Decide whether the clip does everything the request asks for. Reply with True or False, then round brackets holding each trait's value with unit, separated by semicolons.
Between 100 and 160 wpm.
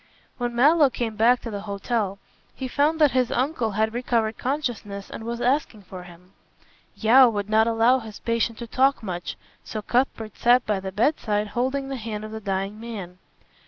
False (185 wpm)